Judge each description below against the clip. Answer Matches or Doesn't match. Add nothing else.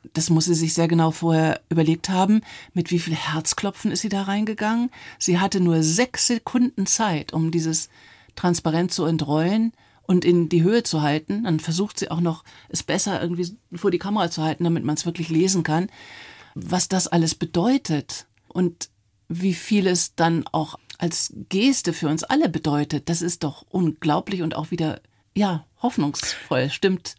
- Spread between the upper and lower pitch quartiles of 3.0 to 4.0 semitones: Matches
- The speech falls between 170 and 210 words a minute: Matches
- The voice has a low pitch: Doesn't match